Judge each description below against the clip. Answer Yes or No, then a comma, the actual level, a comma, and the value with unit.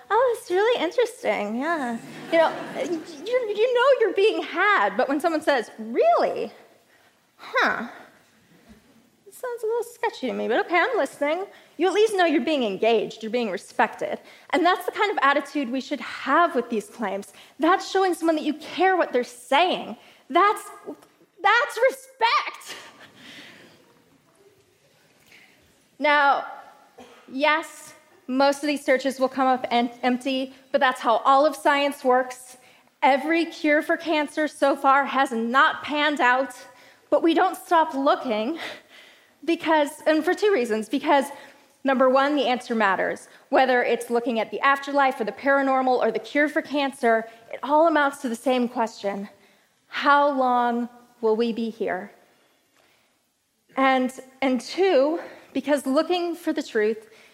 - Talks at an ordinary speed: Yes, average, 150 wpm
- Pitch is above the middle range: Yes, very high, 285 Hz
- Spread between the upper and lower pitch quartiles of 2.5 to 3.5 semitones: No, average, 4.8 semitones